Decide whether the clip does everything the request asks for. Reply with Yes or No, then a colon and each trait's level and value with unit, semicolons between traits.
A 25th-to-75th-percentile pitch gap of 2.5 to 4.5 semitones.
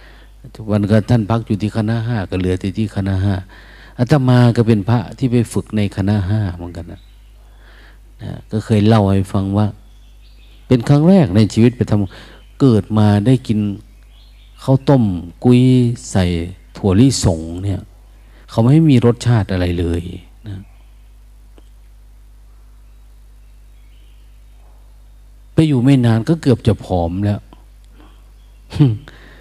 Yes: average, 3.5 semitones